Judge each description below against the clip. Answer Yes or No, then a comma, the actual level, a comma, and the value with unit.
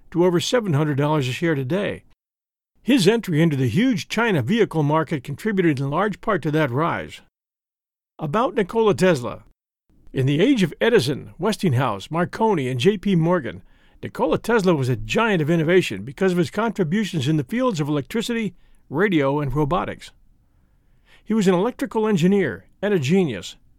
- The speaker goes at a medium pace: Yes, average, 155 wpm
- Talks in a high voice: No, medium, 175 Hz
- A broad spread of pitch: Yes, wide, 5.7 semitones